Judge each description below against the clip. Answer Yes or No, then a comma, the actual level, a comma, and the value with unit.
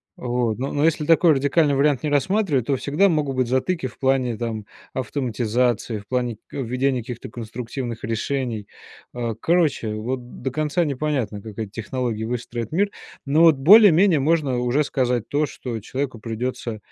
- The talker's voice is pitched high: No, low, 130 Hz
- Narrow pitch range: No, average, 3.8 semitones